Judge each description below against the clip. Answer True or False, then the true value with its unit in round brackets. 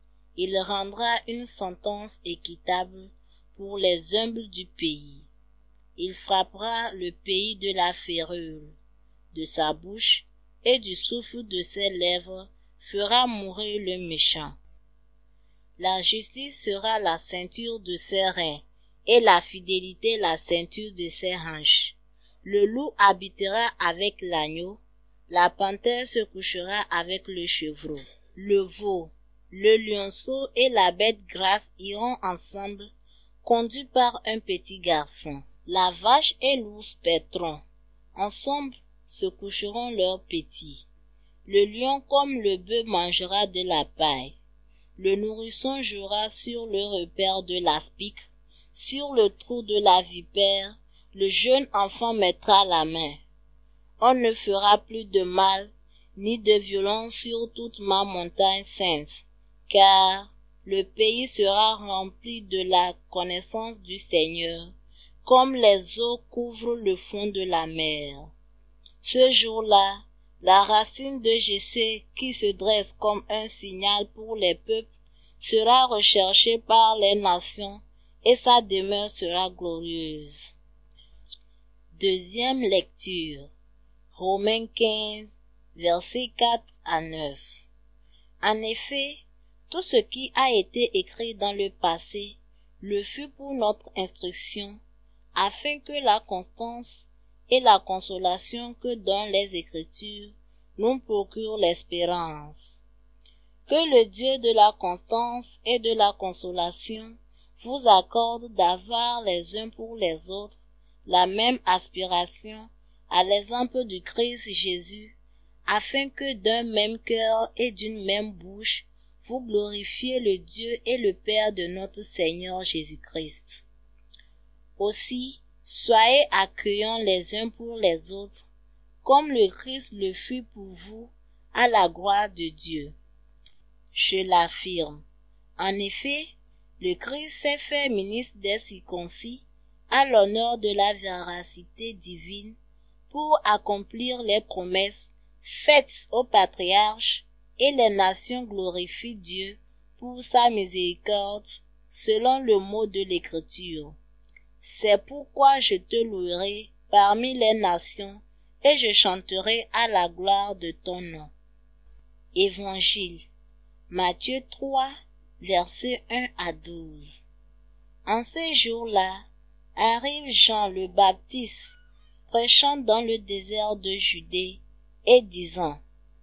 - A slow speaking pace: True (120 wpm)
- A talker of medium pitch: False (200 Hz)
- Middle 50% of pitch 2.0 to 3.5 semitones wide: False (4.4 semitones)